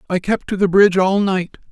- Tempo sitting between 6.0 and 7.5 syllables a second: No, 5.7 syllables/s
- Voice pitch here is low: No, high, 190 Hz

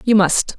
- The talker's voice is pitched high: Yes, high, 205 Hz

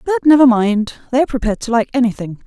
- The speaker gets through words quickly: Yes, fast, 220 wpm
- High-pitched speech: Yes, high, 245 Hz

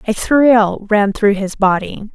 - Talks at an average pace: Yes, average, 170 wpm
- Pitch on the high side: Yes, high, 210 Hz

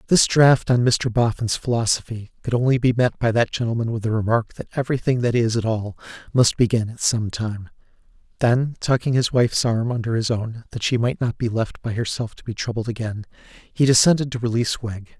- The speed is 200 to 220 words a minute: Yes, fast, 205 wpm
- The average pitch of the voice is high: No, low, 115 Hz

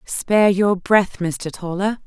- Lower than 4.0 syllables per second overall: Yes, 3.7 syllables/s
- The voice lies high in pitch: Yes, high, 195 Hz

